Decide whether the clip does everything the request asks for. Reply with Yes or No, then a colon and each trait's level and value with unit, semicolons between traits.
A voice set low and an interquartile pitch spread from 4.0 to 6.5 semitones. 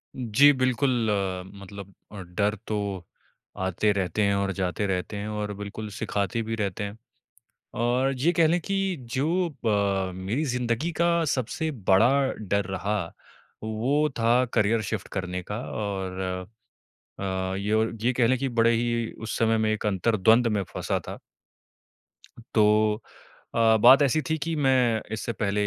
No: low, 110 Hz; average, 3.6 semitones